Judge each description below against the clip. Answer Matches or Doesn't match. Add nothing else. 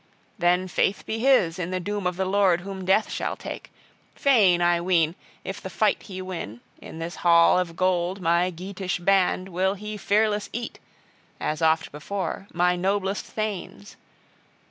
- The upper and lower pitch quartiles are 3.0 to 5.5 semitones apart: Doesn't match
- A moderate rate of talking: Matches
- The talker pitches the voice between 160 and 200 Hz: Matches